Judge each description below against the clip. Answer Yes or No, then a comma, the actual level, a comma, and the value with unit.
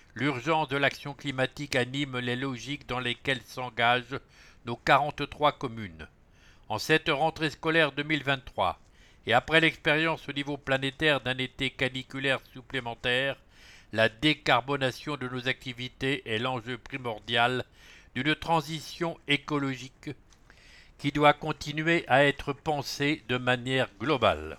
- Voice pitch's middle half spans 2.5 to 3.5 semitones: Yes, average, 3.0 semitones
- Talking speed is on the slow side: Yes, slow, 115 wpm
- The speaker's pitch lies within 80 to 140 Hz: Yes, low, 135 Hz